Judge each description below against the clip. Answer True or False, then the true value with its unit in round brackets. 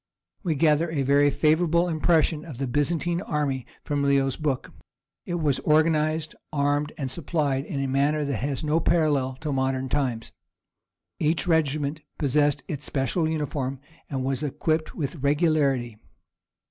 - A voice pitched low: False (145 Hz)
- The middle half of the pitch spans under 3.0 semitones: True (2.5 semitones)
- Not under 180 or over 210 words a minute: False (145 wpm)